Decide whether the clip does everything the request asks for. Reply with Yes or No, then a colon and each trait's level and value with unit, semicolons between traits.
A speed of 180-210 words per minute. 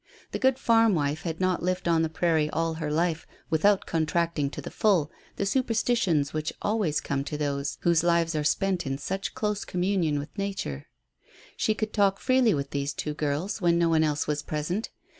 Yes: average, 195 wpm